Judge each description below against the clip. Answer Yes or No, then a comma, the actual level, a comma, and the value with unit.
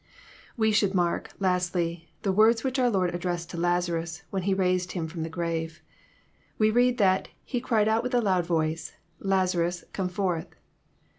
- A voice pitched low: No, medium, 180 Hz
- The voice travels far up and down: No, average, 3.5 semitones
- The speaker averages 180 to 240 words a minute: No, average, 170 wpm